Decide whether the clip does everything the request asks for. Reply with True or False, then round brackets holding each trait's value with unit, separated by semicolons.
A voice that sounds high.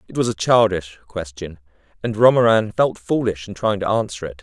False (100 Hz)